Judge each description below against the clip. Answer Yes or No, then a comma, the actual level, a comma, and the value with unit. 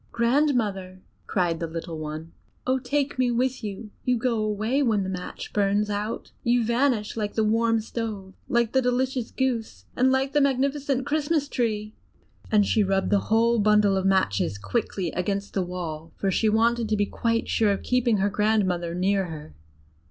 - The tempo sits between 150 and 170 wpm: No, average, 180 wpm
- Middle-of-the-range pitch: No, high, 215 Hz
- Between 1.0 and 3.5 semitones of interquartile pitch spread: No, average, 4.2 semitones